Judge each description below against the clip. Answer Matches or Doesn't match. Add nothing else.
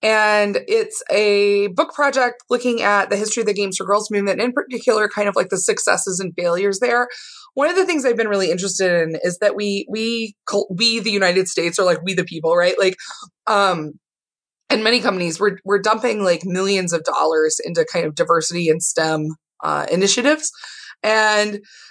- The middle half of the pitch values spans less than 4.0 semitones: Doesn't match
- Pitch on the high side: Matches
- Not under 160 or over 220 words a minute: Matches